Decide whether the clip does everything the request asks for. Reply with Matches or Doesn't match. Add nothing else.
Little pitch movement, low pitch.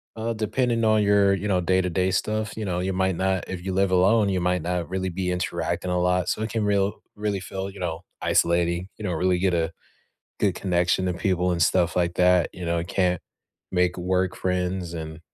Matches